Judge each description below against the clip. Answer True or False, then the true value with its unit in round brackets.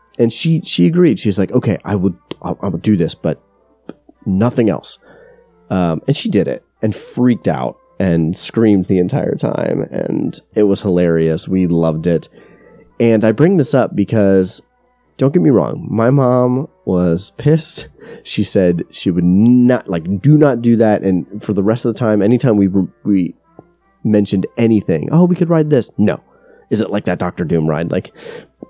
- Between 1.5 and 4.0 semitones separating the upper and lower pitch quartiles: False (5.4 semitones)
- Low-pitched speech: True (105 Hz)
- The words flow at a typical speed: True (180 wpm)